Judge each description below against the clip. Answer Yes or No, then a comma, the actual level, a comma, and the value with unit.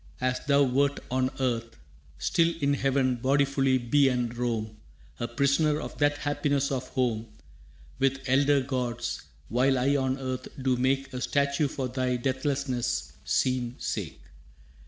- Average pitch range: No, narrow, 2.0 semitones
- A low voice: Yes, low, 130 Hz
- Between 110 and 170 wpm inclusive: Yes, average, 140 wpm